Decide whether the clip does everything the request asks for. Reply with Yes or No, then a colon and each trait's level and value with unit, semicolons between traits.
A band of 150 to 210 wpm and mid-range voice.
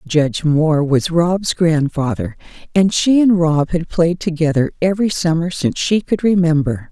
Yes: average, 155 wpm; medium, 165 Hz